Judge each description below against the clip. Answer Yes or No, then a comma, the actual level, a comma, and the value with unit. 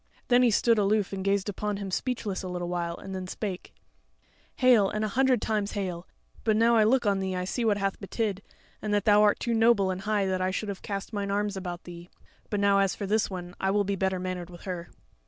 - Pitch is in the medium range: No, high, 200 Hz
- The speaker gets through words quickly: Yes, fast, 245 wpm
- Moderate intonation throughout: No, narrow, 2.3 semitones